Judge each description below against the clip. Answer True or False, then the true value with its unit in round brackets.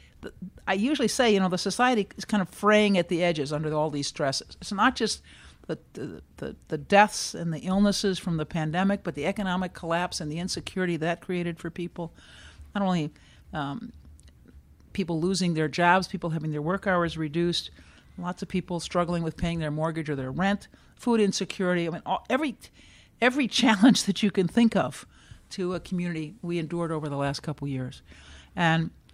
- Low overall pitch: False (175 Hz)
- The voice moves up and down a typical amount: True (4.0 semitones)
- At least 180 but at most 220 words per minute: True (185 wpm)